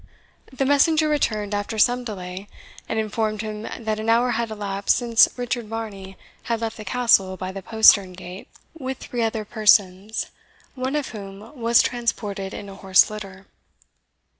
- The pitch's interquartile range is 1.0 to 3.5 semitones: Yes, average, 3.2 semitones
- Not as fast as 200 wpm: Yes, average, 165 wpm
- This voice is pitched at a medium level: No, high, 215 Hz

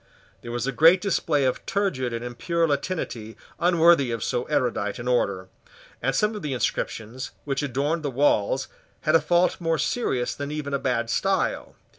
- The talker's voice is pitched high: No, medium, 140 Hz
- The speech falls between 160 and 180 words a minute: Yes, average, 175 wpm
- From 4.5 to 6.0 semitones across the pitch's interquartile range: Yes, average, 5.2 semitones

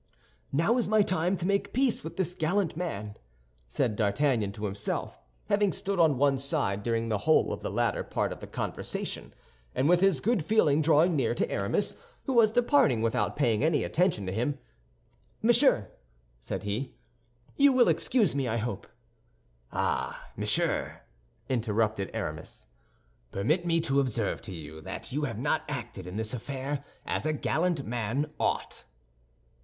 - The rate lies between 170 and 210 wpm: No, average, 160 wpm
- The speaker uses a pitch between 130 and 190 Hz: Yes, medium, 140 Hz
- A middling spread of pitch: No, wide, 8.2 semitones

